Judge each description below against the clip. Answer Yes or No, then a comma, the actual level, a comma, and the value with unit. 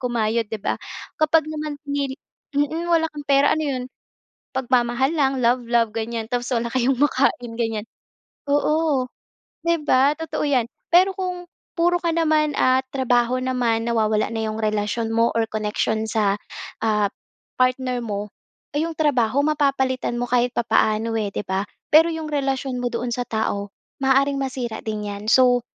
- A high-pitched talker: Yes, very high, 250 Hz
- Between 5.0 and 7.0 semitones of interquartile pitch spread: No, average, 4.1 semitones